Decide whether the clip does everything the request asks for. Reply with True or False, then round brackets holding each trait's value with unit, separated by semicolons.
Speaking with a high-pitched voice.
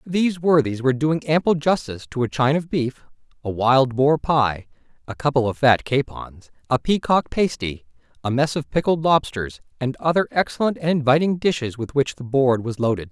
False (140 Hz)